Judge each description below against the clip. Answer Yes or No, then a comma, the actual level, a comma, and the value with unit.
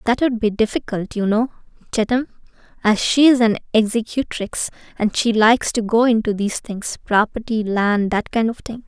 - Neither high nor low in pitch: No, high, 220 Hz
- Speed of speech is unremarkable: Yes, average, 170 wpm